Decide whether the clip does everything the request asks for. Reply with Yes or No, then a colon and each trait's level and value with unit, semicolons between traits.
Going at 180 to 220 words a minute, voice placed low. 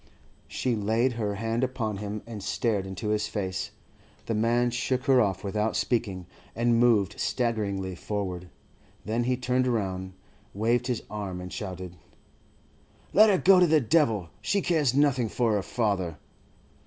No: average, 155 wpm; low, 110 Hz